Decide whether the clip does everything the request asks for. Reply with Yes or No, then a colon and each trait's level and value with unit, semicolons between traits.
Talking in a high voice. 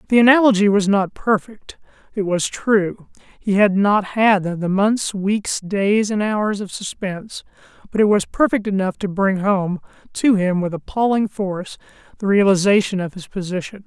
Yes: high, 200 Hz